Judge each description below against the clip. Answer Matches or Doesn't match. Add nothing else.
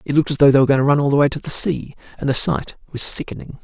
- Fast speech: Matches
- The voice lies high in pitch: Doesn't match